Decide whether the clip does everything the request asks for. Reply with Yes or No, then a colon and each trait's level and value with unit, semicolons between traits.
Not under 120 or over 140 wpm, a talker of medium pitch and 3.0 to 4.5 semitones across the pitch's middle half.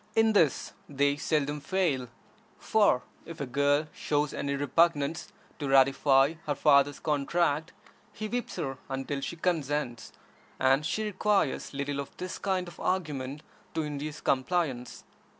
Yes: slow, 135 wpm; medium, 145 Hz; average, 3.6 semitones